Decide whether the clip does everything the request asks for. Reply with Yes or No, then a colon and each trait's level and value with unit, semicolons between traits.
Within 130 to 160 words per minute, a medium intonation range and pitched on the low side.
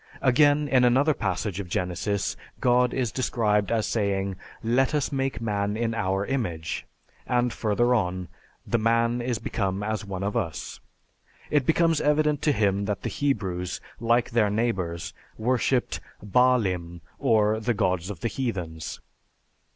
Yes: average, 150 wpm; average, 4.4 semitones; low, 110 Hz